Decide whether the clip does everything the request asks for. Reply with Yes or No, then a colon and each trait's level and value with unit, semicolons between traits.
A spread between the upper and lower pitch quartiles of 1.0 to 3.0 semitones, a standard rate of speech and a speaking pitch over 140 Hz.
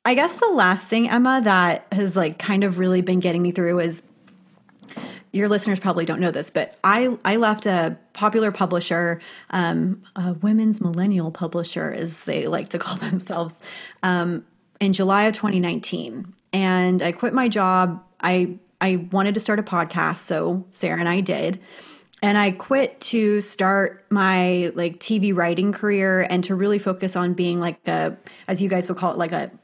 Yes: average, 2.7 semitones; average, 180 wpm; medium, 185 Hz